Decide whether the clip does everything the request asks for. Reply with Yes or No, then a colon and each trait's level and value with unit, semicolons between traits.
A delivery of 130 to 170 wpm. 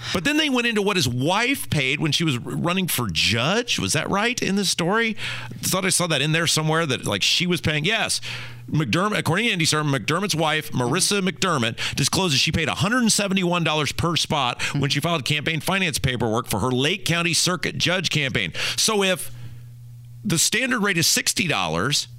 No: fast, 205 wpm